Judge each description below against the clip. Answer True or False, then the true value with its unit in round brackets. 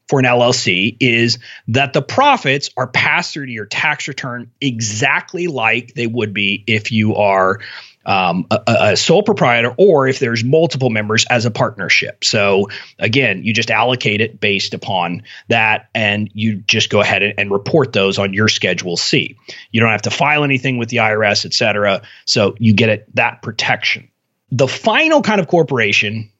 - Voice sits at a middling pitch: False (115 Hz)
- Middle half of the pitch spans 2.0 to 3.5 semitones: False (4.0 semitones)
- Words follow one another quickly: False (180 wpm)